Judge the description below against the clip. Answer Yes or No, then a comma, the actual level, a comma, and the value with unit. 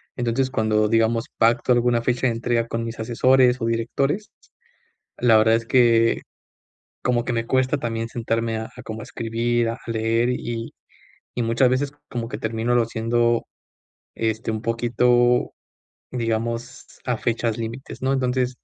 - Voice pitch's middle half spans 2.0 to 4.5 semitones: No, narrow, 1.4 semitones